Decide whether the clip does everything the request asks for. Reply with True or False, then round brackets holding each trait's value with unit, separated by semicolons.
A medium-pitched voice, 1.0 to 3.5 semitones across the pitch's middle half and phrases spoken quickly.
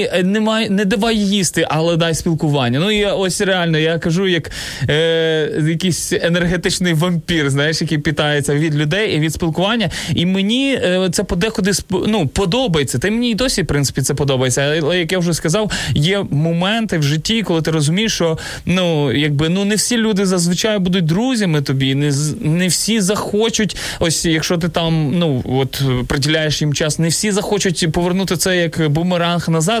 False (170 Hz; 4.2 semitones; 175 wpm)